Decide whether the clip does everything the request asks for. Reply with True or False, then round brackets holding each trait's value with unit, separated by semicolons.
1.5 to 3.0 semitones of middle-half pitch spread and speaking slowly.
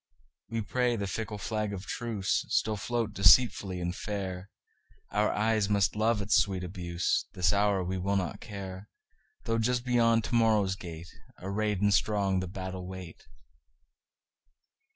True (2.7 semitones; 130 wpm)